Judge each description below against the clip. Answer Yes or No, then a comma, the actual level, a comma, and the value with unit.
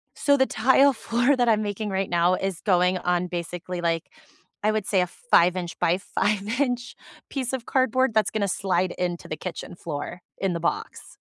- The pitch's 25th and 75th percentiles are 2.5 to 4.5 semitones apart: No, average, 5.1 semitones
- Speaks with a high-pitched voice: Yes, high, 195 Hz